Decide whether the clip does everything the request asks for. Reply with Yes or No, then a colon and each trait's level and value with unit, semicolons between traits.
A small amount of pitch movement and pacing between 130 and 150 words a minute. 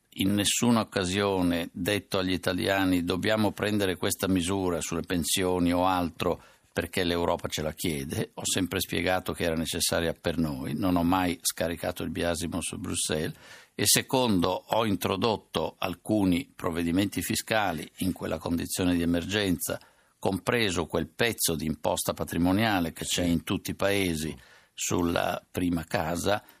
Yes: narrow, 2.3 semitones; average, 140 wpm